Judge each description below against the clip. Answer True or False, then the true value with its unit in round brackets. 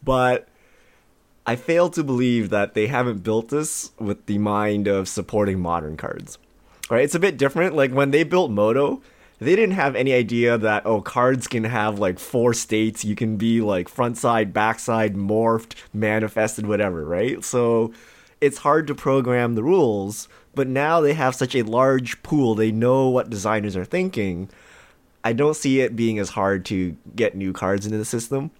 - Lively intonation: False (3.9 semitones)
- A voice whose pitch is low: True (115 Hz)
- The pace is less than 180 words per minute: False (185 wpm)